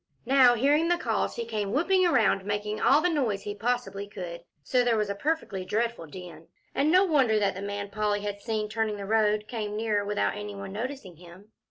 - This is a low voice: No, high, 210 Hz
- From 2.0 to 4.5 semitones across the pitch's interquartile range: Yes, average, 3.7 semitones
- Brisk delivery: Yes, fast, 210 wpm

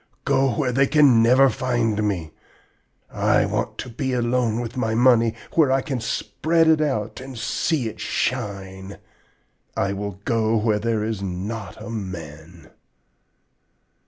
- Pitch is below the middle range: Yes, low, 115 Hz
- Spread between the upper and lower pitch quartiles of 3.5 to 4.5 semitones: Yes, average, 4.0 semitones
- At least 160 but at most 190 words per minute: No, average, 145 wpm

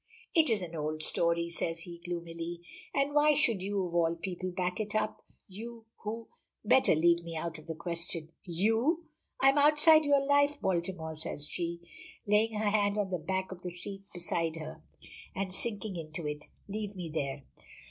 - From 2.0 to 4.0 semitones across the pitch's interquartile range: No, average, 4.4 semitones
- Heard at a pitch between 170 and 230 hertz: Yes, medium, 185 Hz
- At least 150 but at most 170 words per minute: No, average, 185 wpm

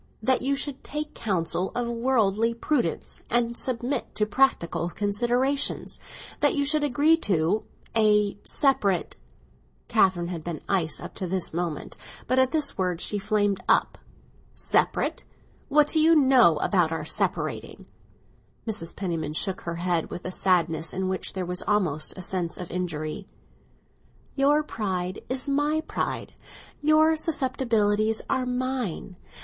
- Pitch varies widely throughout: Yes, wide, 6.6 semitones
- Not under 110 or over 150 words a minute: Yes, average, 140 wpm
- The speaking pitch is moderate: No, high, 210 Hz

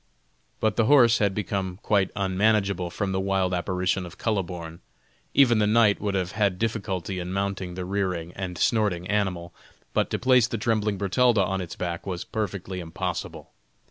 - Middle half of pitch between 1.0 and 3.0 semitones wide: Yes, average, 2.7 semitones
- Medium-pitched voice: No, very low, 95 Hz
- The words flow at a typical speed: Yes, average, 170 wpm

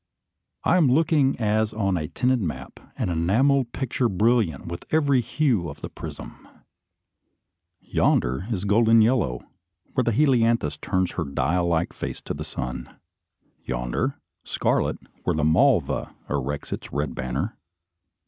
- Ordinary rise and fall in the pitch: No, wide, 7.7 semitones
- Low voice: Yes, low, 105 Hz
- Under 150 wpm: Yes, average, 140 wpm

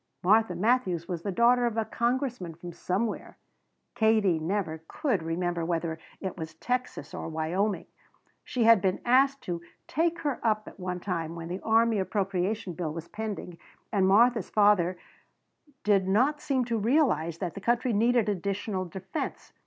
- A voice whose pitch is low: No, high, 200 Hz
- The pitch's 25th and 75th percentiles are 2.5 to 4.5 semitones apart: No, average, 4.9 semitones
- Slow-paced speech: No, average, 160 wpm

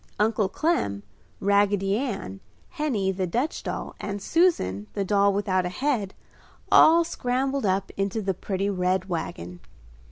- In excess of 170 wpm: No, slow, 135 wpm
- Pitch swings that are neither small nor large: Yes, average, 4.8 semitones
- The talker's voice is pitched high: Yes, high, 200 Hz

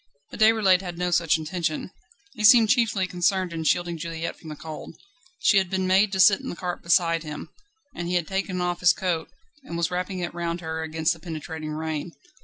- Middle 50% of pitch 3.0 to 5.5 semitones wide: No, narrow, 2.5 semitones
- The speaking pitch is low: No, medium, 175 Hz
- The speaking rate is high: Yes, fast, 210 wpm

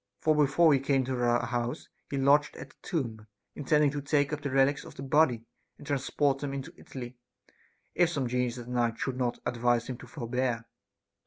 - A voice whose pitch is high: No, low, 135 Hz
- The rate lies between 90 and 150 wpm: No, average, 195 wpm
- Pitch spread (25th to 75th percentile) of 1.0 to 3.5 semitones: Yes, average, 2.8 semitones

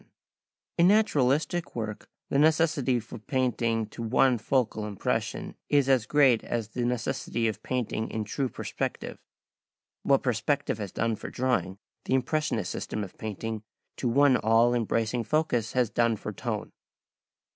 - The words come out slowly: No, average, 150 wpm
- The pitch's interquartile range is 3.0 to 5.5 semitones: Yes, average, 3.5 semitones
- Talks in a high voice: No, low, 120 Hz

